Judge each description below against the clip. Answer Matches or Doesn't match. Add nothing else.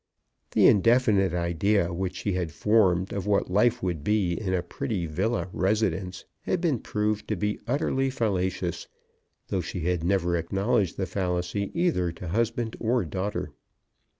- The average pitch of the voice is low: Matches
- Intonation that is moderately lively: Matches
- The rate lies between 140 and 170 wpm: Matches